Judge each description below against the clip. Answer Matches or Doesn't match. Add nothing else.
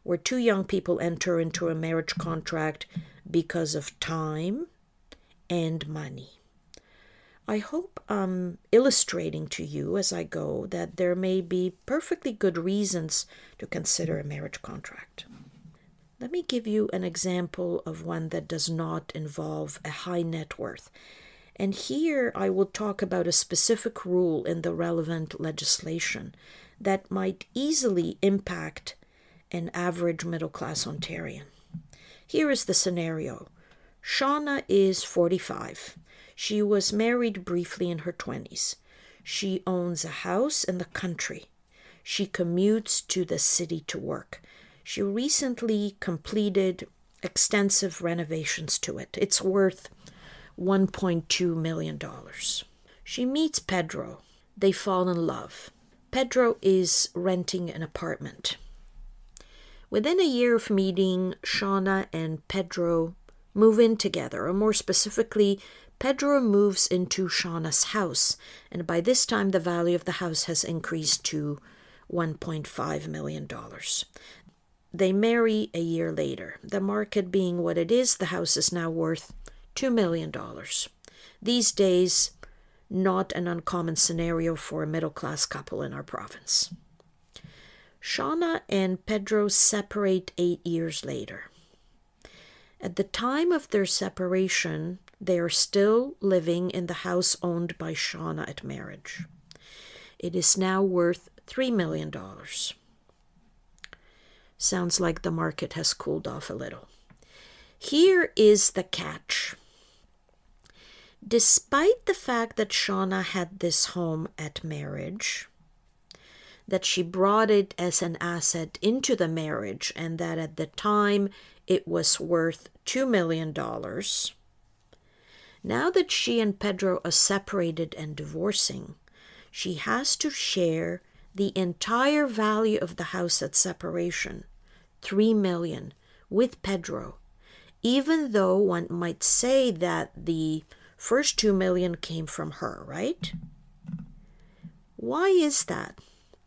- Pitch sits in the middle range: Matches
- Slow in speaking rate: Matches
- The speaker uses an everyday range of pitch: Matches